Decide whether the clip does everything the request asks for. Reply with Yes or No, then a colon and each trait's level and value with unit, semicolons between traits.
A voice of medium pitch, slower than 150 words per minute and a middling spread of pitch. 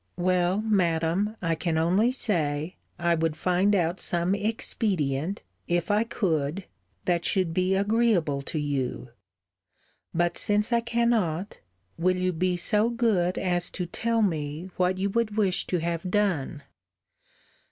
Yes: medium, 180 Hz; average, 140 wpm; average, 3.8 semitones